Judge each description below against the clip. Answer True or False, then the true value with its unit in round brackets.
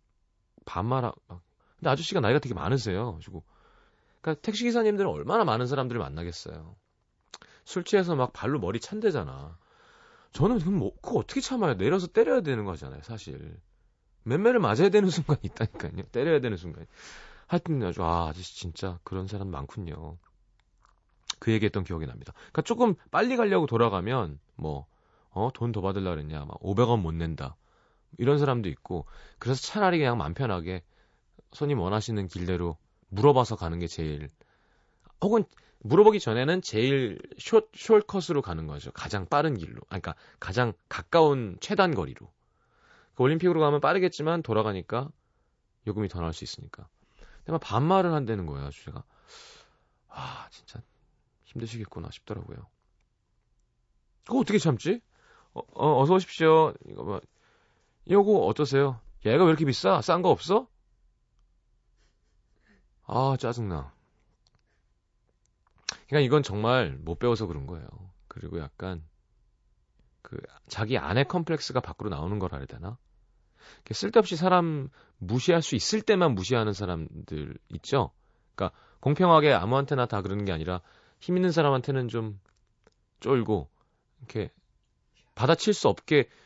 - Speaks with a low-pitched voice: True (115 Hz)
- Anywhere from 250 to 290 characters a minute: False (310 characters per minute)